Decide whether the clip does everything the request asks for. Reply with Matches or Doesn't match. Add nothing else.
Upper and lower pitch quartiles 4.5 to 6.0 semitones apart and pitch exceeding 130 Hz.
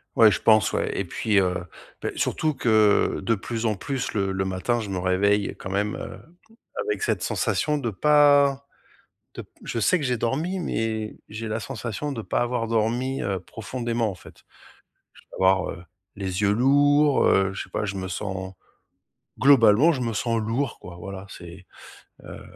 Doesn't match